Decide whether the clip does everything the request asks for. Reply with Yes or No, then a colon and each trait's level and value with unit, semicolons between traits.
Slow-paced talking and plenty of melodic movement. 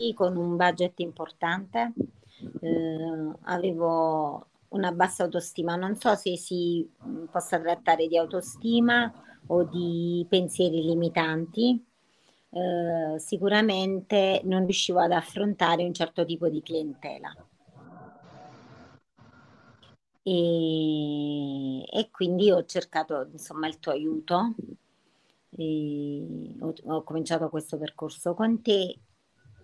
No: slow, 100 wpm; average, 3.0 semitones